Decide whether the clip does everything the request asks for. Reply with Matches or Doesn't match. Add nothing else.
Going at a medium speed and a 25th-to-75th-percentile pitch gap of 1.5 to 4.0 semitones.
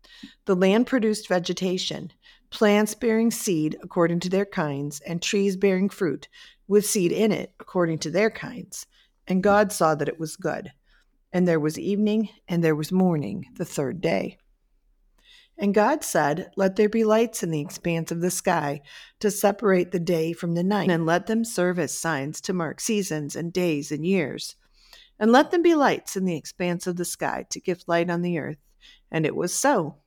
Matches